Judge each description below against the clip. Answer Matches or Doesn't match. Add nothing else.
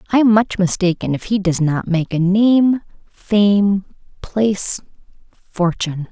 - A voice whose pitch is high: Matches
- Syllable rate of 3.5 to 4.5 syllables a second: Matches